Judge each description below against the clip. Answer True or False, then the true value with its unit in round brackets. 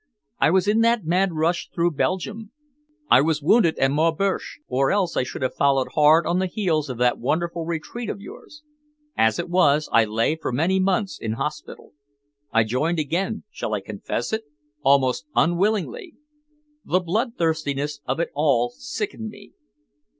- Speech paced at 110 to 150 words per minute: False (165 wpm)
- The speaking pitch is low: False (160 Hz)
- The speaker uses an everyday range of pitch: False (5.7 semitones)